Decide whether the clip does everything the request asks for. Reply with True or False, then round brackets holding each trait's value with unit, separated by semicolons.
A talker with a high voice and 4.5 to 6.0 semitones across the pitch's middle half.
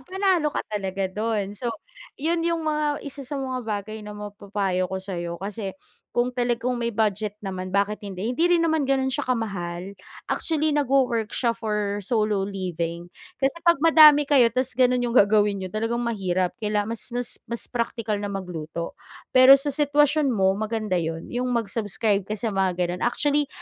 True (220 Hz; 5.1 semitones)